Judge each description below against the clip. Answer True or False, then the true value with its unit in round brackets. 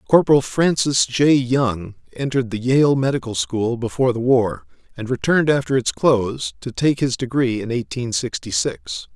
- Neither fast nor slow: True (165 wpm)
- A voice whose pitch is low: True (125 Hz)